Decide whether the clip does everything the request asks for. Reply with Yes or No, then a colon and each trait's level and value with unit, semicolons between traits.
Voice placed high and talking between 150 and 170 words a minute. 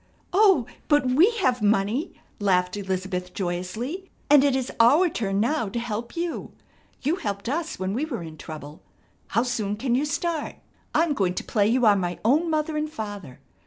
No: high, 235 Hz; average, 180 wpm